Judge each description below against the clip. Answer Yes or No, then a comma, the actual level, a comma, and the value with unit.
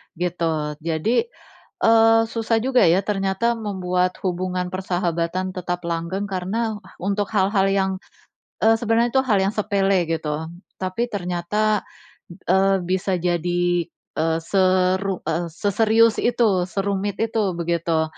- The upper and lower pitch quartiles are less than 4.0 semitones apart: Yes, average, 3.1 semitones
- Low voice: No, high, 190 Hz